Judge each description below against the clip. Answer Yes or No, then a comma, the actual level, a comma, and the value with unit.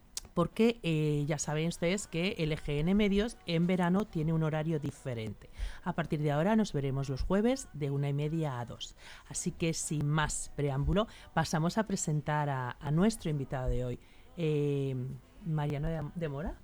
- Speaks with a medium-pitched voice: Yes, medium, 155 Hz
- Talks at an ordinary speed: Yes, average, 175 wpm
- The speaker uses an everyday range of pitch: Yes, average, 3.5 semitones